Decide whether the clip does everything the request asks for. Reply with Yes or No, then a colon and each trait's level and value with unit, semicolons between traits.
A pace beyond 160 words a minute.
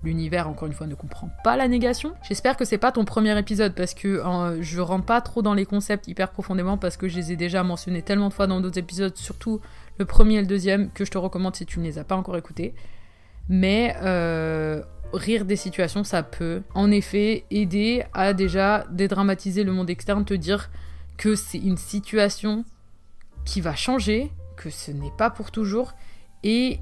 Yes: average, 205 wpm